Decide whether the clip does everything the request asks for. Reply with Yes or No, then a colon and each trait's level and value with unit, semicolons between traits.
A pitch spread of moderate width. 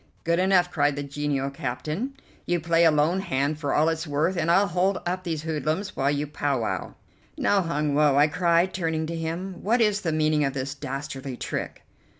Yes: average, 3.4 semitones